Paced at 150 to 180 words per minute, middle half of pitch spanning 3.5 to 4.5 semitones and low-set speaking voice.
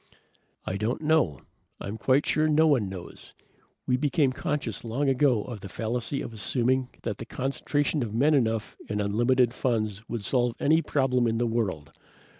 Yes: average, 170 wpm; average, 3.9 semitones; low, 125 Hz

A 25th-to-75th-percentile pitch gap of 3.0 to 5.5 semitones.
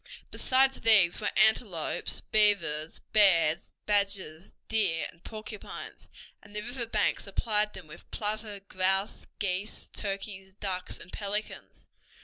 No: narrow, 2.4 semitones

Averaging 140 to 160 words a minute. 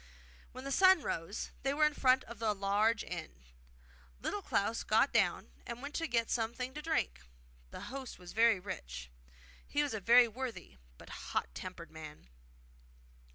No: average, 170 wpm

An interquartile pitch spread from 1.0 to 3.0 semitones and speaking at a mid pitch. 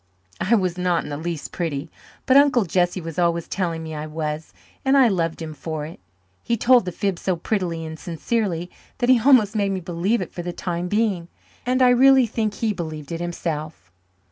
No: average, 5.0 semitones; medium, 175 Hz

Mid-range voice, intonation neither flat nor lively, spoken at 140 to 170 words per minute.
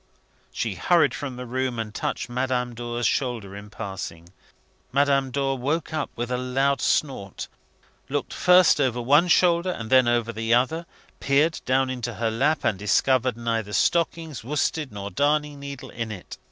No: low, 130 Hz; average, 3.7 semitones; average, 165 wpm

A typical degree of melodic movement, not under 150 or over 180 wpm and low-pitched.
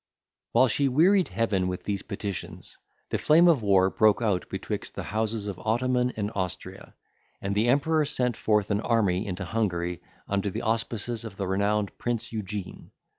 Yes: average, 3.5 semitones; average, 170 wpm; low, 105 Hz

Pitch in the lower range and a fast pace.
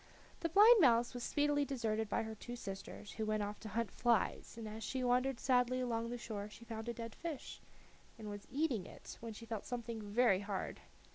No: high, 230 Hz; fast, 210 wpm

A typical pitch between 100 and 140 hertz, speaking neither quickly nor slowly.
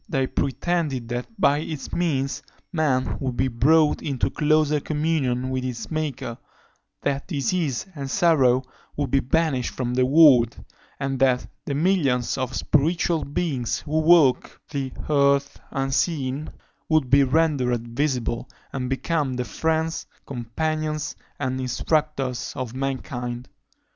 No: low, 135 Hz; slow, 130 wpm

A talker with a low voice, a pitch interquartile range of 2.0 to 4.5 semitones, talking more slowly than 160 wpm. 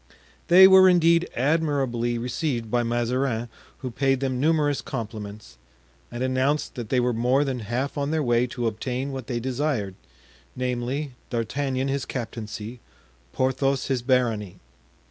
Yes: low, 130 Hz; average, 2.8 semitones; average, 140 wpm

